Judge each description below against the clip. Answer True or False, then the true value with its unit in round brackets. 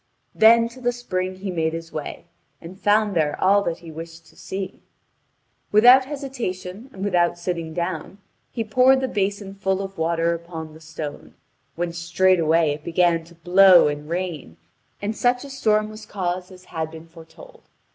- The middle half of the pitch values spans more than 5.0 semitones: False (3.9 semitones)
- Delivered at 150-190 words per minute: True (170 wpm)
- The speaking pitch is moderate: True (180 Hz)